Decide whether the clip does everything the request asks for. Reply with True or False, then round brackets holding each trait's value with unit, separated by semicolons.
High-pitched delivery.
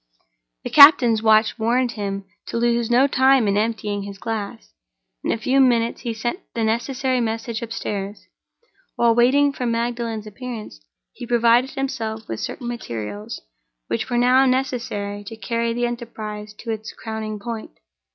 True (230 Hz)